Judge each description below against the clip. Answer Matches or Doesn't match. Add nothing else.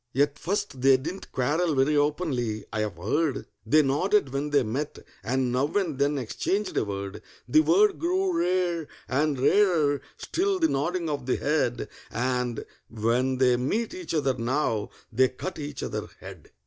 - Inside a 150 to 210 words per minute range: Matches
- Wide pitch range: Matches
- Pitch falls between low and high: Matches